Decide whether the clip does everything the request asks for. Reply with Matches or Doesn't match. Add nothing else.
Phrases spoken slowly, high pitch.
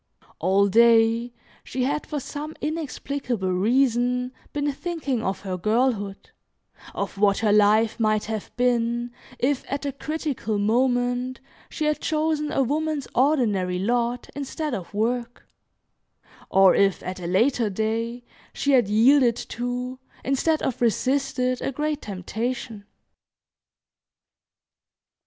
Matches